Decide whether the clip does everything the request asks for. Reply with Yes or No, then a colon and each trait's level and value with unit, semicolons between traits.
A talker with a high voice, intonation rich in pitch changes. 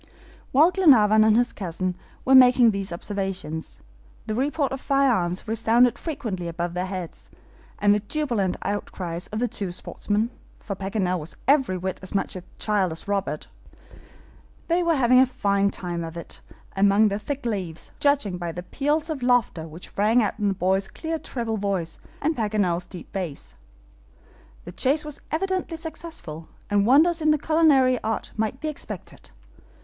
Yes: high, 210 Hz; wide, 6.2 semitones